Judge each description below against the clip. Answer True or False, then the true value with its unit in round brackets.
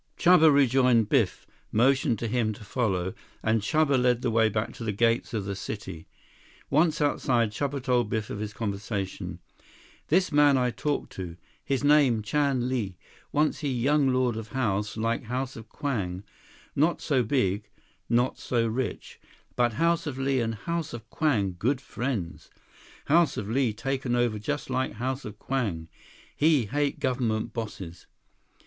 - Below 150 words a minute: False (160 wpm)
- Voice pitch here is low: True (120 Hz)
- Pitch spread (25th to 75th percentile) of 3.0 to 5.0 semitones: True (4.3 semitones)